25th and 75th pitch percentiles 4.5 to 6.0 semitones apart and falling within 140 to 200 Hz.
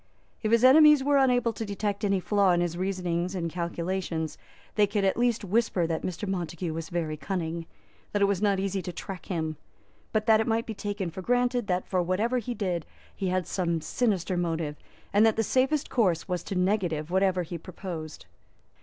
No: average, 3.9 semitones; high, 190 Hz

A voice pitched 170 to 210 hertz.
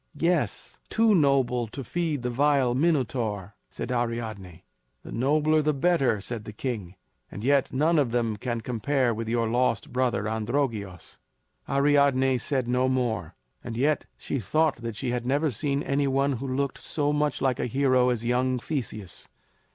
No: low, 130 Hz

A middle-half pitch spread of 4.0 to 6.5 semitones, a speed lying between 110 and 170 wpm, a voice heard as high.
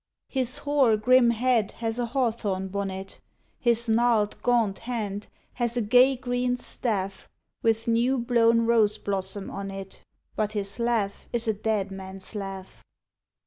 No: average, 3.2 semitones; average, 145 wpm; high, 225 Hz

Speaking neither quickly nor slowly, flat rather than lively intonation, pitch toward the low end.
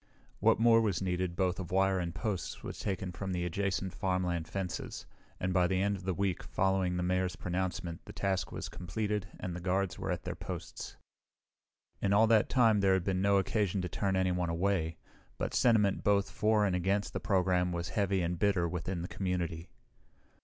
Yes: average, 190 wpm; narrow, 1.9 semitones; very low, 95 Hz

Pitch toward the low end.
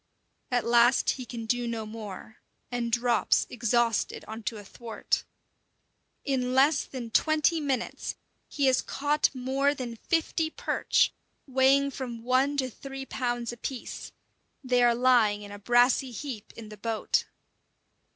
No: high, 245 Hz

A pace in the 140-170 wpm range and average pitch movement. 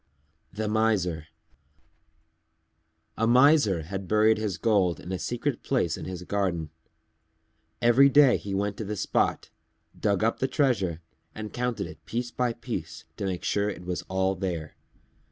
Yes: average, 155 wpm; average, 4.3 semitones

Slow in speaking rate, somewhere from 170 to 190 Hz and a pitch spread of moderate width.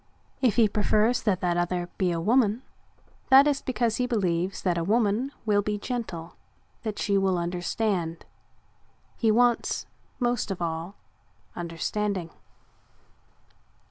No: slow, 130 wpm; high, 205 Hz; average, 4.8 semitones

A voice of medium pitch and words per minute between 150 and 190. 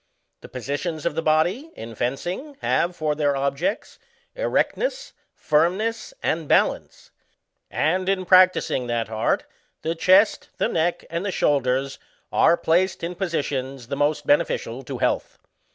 No: medium, 160 Hz; slow, 135 wpm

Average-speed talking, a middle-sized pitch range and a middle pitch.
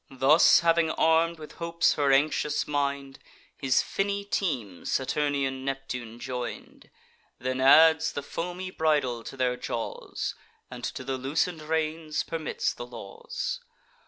No: slow, 130 wpm; average, 3.7 semitones; medium, 145 Hz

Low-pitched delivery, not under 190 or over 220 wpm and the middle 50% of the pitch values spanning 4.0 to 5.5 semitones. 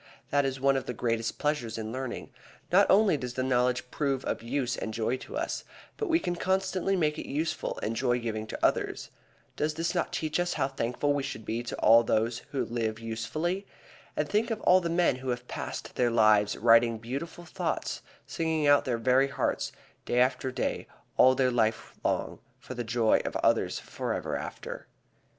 Yes: low, 130 Hz; average, 195 wpm; average, 5.0 semitones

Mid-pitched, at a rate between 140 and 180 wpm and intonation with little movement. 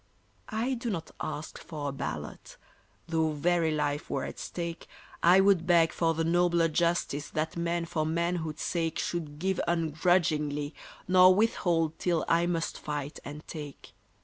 Yes: medium, 165 Hz; average, 150 wpm; narrow, 2.1 semitones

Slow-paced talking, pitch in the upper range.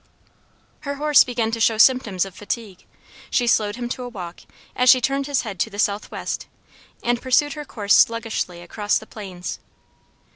No: average, 175 wpm; high, 230 Hz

